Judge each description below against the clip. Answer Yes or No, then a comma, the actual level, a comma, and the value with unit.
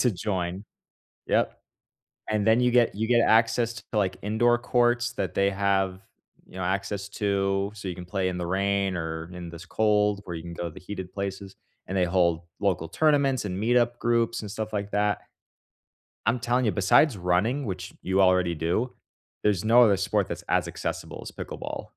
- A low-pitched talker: Yes, low, 100 Hz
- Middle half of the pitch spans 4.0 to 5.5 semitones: No, average, 3.5 semitones